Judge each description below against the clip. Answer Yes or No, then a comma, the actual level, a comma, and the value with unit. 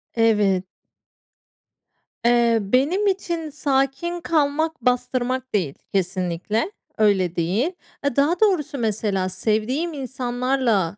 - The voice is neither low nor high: No, high, 245 Hz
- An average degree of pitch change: No, wide, 5.9 semitones